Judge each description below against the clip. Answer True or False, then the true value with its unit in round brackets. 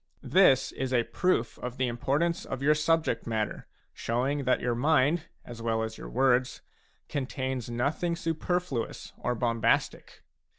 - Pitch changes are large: False (4.4 semitones)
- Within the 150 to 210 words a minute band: False (140 wpm)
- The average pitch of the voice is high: False (130 Hz)